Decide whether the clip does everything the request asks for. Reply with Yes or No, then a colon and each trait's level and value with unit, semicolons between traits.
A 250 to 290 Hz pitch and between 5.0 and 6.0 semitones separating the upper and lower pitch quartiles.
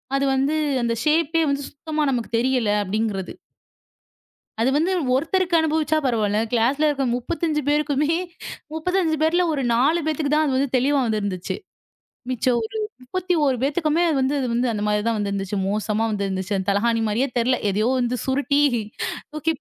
Yes: very high, 265 Hz; wide, 5.4 semitones